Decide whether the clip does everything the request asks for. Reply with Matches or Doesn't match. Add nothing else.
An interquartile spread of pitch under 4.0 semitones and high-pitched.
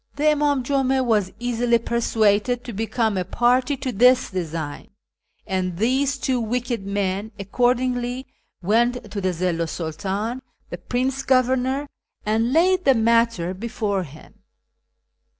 Doesn't match